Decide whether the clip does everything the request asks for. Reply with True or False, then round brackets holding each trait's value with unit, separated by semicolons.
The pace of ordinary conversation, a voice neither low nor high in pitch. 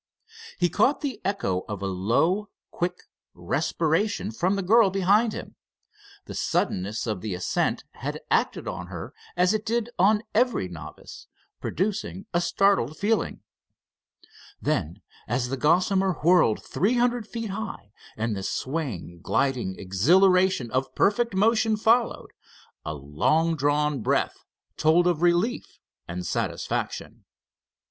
False (130 wpm; 175 Hz)